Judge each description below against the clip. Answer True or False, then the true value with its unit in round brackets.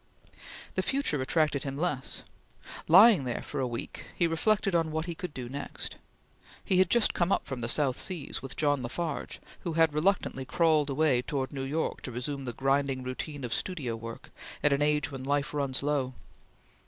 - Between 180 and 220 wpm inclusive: True (190 wpm)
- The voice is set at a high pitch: False (145 Hz)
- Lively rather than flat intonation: False (3.7 semitones)